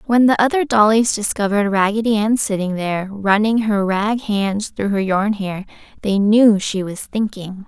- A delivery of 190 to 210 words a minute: No, average, 170 wpm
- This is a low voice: No, high, 210 Hz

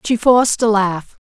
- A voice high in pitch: Yes, high, 215 Hz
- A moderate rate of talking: Yes, average, 190 wpm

